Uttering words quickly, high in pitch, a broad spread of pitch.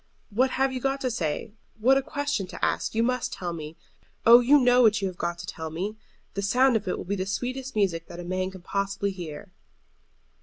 Yes: fast, 230 wpm; high, 200 Hz; wide, 5.7 semitones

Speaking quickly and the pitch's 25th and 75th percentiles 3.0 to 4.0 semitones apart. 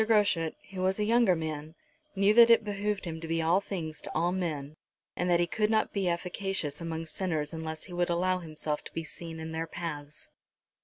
Yes: fast, 210 wpm; average, 3.3 semitones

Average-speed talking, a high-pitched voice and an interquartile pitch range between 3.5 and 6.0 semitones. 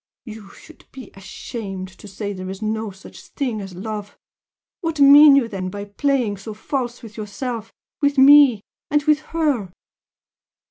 Yes: average, 155 wpm; high, 220 Hz; wide, 5.6 semitones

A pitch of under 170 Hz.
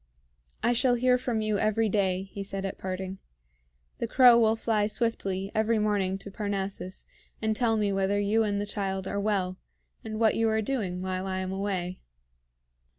No: high, 205 Hz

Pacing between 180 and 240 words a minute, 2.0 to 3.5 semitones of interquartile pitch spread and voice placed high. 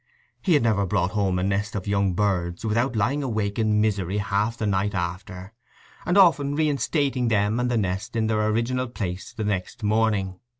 No: average, 185 wpm; average, 3.1 semitones; low, 105 Hz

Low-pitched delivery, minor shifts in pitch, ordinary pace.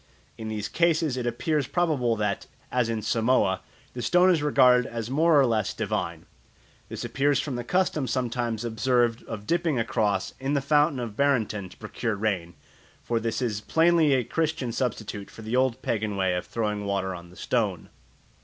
No: low, 120 Hz; average, 4.5 semitones; average, 180 wpm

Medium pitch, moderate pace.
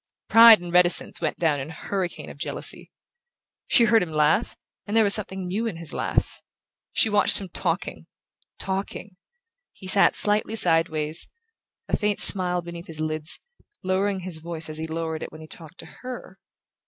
Yes: medium, 180 Hz; average, 165 wpm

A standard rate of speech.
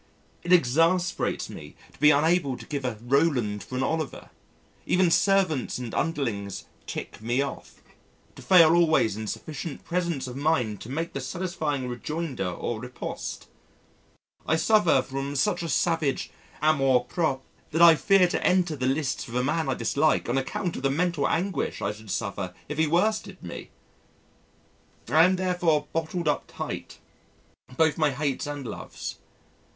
Yes: average, 160 wpm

